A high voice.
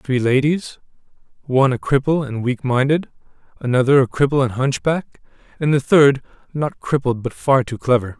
No: low, 130 Hz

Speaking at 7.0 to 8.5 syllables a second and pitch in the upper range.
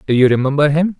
No: 7.2 syllables/s; medium, 145 Hz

